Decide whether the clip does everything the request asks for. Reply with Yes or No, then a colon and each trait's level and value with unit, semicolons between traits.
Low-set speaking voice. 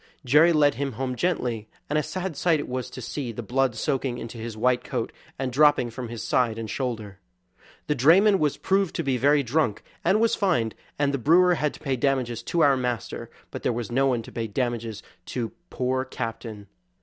Yes: low, 130 Hz